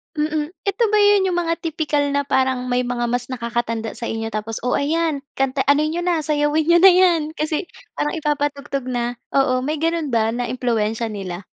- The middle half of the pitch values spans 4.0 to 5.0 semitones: Yes, average, 4.7 semitones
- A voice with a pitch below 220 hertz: No, very high, 285 Hz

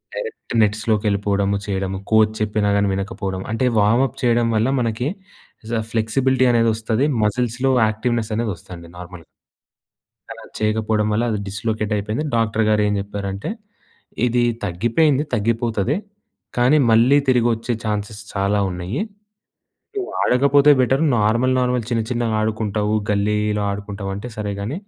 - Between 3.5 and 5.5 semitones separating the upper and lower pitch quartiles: No, average, 2.7 semitones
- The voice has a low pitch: Yes, low, 110 Hz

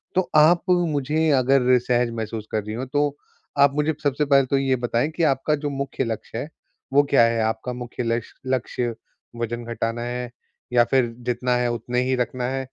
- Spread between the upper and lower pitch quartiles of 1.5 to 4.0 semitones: Yes, average, 2.9 semitones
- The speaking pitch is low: Yes, low, 125 Hz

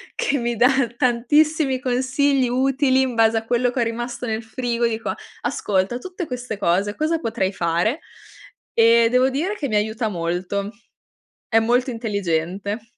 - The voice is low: No, high, 235 Hz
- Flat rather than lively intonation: No, average, 3.4 semitones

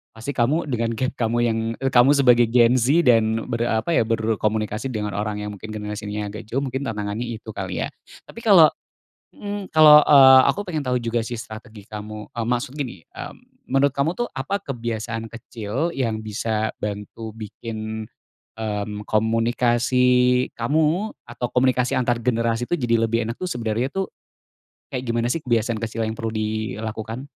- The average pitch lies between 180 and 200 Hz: No, low, 115 Hz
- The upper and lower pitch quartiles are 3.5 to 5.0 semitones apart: No, average, 2.7 semitones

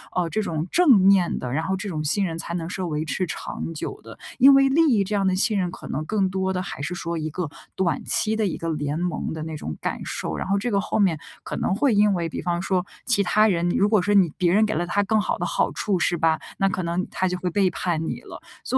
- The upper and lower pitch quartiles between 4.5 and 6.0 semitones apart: No, average, 3.4 semitones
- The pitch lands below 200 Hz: Yes, medium, 185 Hz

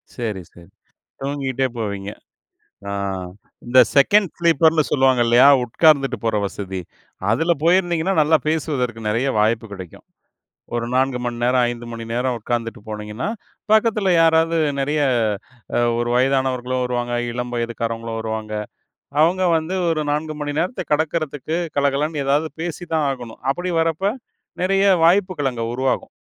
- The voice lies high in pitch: No, low, 135 Hz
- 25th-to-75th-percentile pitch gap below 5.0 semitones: No, wide, 5.4 semitones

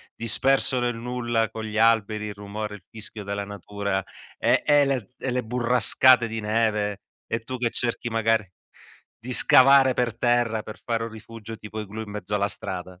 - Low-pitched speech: Yes, low, 110 Hz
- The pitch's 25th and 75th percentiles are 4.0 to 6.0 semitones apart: No, narrow, 2.6 semitones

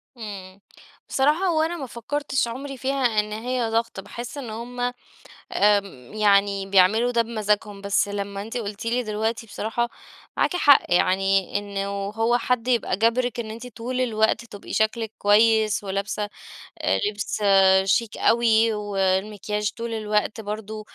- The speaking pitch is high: Yes, high, 220 Hz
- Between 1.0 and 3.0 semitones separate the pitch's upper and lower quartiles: Yes, average, 2.7 semitones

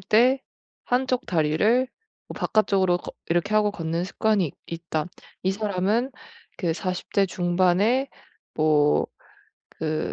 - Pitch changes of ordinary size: Yes, average, 4.4 semitones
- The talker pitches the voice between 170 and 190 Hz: Yes, medium, 185 Hz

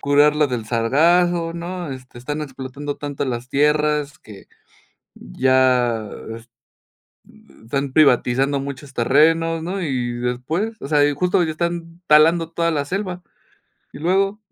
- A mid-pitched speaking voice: Yes, medium, 145 Hz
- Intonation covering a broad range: No, average, 4.3 semitones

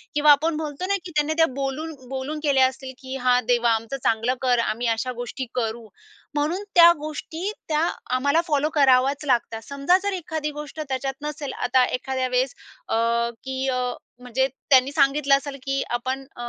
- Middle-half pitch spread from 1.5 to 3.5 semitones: Yes, average, 2.9 semitones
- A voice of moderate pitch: No, very high, 275 Hz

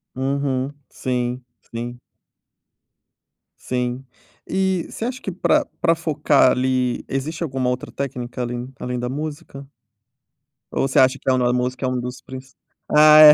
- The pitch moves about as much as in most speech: Yes, average, 3.2 semitones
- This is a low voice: Yes, low, 130 Hz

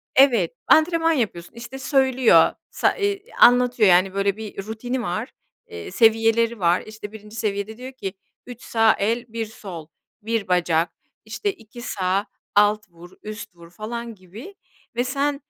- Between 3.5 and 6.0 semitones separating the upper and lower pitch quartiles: Yes, average, 3.9 semitones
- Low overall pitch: No, high, 220 Hz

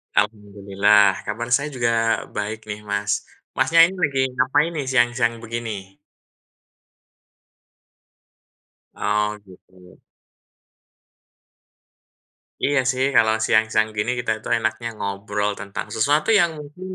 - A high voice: No, low, 110 Hz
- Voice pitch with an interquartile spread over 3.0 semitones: Yes, average, 3.9 semitones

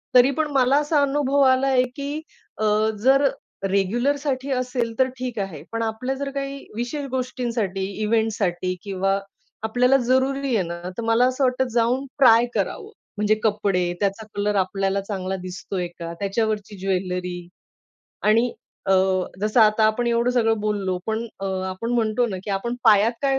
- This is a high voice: Yes, high, 225 Hz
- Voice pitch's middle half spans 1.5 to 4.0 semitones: No, average, 4.4 semitones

